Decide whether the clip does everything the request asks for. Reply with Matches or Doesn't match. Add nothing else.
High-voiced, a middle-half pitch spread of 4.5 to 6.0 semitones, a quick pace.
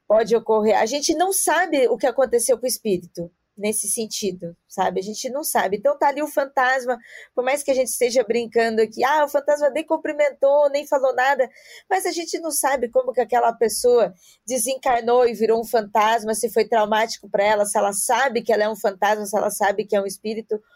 Matches